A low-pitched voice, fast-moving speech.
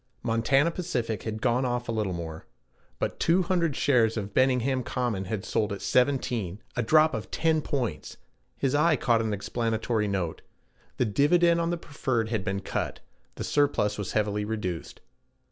No: low, 120 Hz; average, 160 wpm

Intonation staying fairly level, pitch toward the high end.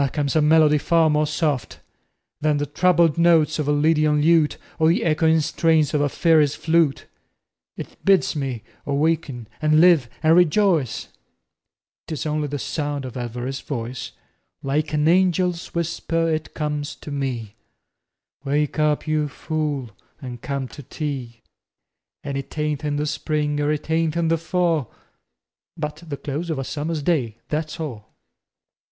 No: narrow, 2.2 semitones; medium, 150 Hz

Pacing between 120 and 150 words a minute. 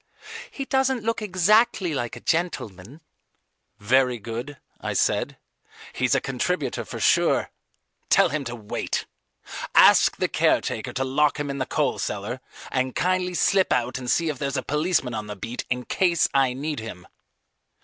No: average, 160 wpm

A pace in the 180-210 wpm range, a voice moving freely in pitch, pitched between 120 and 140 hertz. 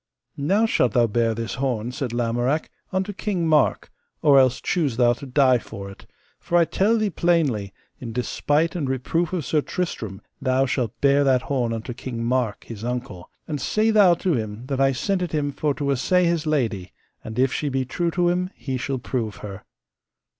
Yes: average, 195 wpm; wide, 5.7 semitones; low, 135 Hz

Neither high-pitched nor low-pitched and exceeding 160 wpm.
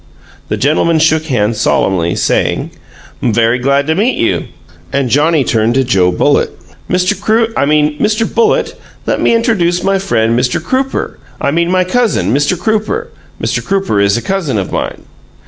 Yes: medium, 155 Hz; average, 170 wpm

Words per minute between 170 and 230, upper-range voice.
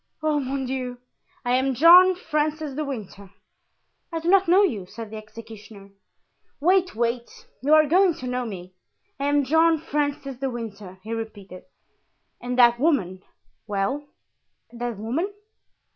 No: average, 145 wpm; very high, 255 Hz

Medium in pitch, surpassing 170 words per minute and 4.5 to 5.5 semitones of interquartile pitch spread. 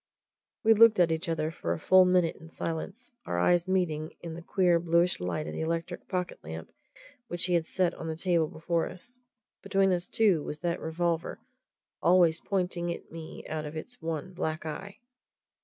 No: medium, 170 Hz; average, 190 wpm; narrow, 2.4 semitones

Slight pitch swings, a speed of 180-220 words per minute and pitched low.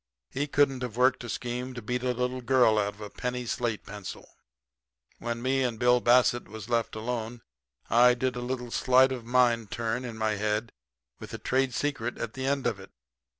Yes: narrow, 1.9 semitones; average, 200 wpm; low, 120 Hz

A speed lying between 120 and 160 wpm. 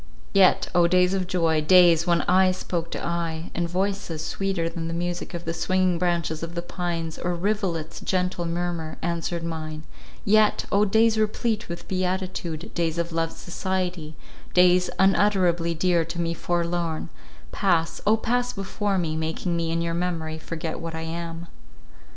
Yes: average, 150 wpm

